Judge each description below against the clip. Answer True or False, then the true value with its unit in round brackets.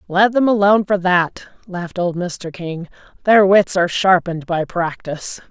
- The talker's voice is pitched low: False (185 Hz)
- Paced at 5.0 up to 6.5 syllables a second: False (4.8 syllables/s)